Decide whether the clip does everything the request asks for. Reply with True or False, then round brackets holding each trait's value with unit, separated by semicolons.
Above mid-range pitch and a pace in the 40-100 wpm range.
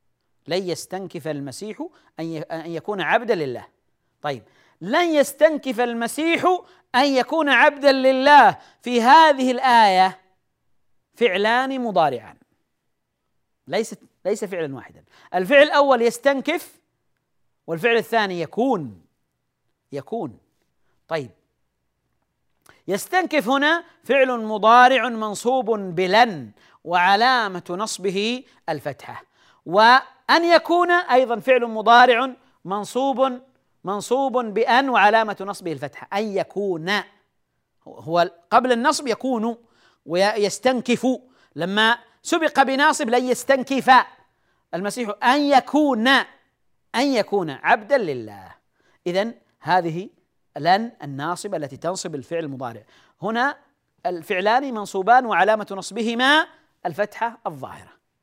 True (230 Hz; 90 wpm)